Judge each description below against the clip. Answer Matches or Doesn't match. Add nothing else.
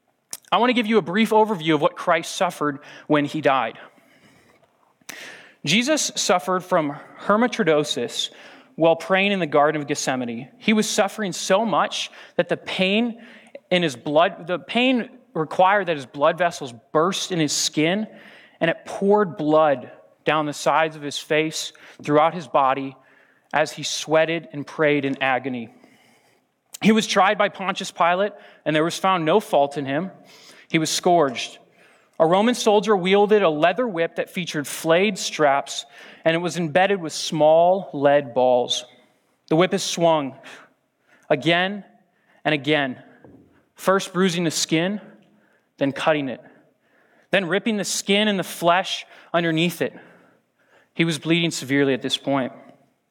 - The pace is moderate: Matches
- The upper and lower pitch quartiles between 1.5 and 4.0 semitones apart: Doesn't match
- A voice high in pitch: Doesn't match